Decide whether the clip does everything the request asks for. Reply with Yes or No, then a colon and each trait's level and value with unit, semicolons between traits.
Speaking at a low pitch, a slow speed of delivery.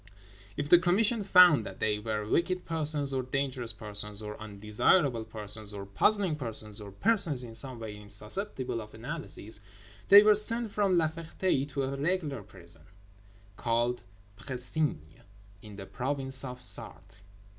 No: low, 130 Hz; average, 145 wpm